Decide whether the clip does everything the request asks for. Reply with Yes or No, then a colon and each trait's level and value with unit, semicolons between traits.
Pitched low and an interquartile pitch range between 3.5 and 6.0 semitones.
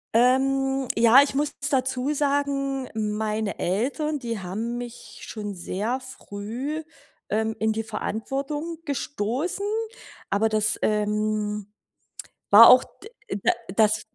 No: high, 235 Hz; average, 4.2 semitones